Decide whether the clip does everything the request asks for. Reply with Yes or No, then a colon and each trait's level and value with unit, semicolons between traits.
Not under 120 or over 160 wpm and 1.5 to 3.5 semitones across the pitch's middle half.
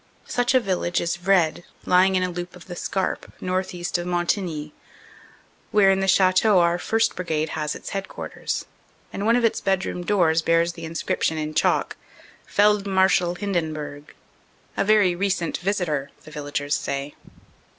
Yes: average, 155 wpm; average, 2.9 semitones